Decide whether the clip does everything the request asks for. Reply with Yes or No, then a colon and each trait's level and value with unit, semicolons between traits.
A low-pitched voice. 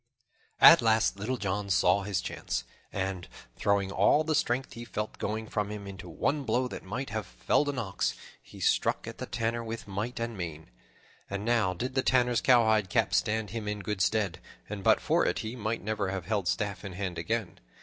Yes: low, 105 Hz